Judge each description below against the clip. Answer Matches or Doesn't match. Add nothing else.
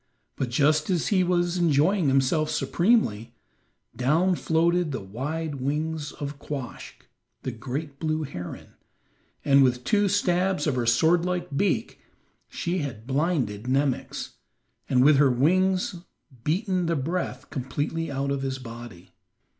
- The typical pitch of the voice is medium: Matches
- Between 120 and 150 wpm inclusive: Matches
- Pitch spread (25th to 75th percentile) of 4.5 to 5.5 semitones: Matches